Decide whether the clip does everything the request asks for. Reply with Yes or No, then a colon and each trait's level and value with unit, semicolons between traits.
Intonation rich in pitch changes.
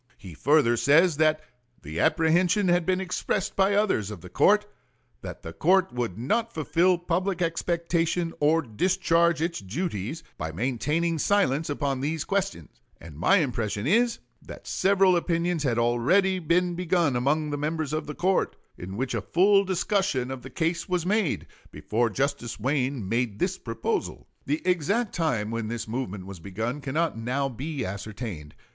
Yes: wide, 7.0 semitones